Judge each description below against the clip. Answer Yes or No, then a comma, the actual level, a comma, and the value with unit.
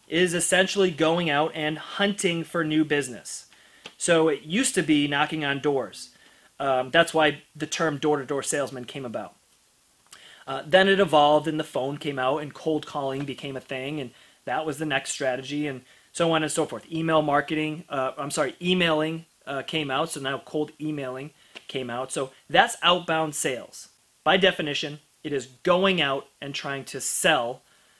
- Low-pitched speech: No, medium, 150 Hz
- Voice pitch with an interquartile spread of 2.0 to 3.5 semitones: Yes, average, 2.8 semitones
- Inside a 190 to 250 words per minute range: No, average, 180 wpm